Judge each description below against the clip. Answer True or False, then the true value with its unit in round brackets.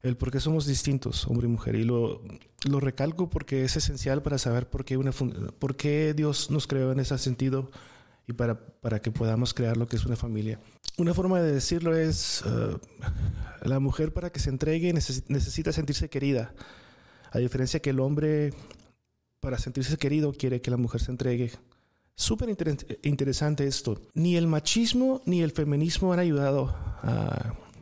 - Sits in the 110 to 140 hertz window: True (135 Hz)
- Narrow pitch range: False (3.9 semitones)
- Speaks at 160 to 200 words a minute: True (175 wpm)